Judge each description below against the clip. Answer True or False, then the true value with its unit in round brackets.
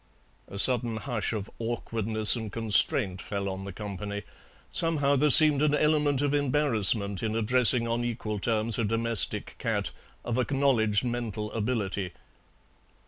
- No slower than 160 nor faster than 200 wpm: False (140 wpm)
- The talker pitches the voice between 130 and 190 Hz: False (115 Hz)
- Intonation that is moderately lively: True (3.5 semitones)